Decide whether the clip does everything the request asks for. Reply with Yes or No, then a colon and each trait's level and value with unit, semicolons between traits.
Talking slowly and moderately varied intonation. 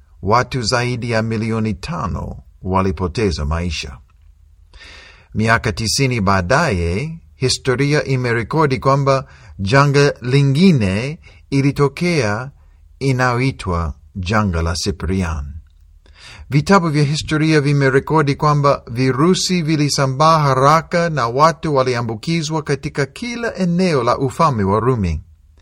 No: slow, 85 wpm; wide, 7.3 semitones